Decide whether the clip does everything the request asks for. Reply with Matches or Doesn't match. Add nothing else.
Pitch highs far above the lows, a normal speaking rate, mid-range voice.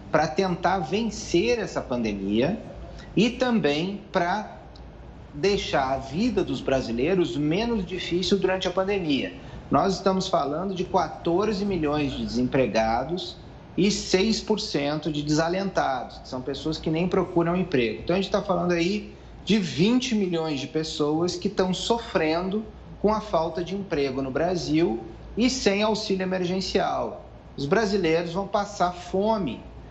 Doesn't match